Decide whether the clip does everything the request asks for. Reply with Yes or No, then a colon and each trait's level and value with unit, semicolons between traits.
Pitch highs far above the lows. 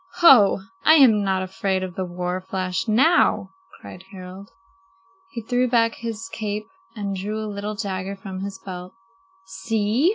No: average, 3.0 semitones